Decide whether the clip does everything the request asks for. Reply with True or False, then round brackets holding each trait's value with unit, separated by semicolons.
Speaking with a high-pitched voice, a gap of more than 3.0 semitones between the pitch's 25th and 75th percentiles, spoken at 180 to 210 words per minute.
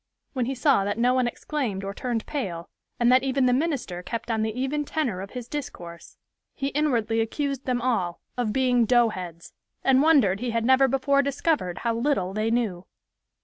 True (245 Hz; 4.1 semitones; 190 wpm)